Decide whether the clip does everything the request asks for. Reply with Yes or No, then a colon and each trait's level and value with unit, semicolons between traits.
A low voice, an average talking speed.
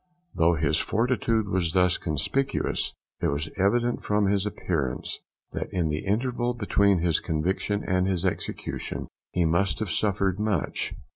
Yes: very low, 95 Hz; average, 145 wpm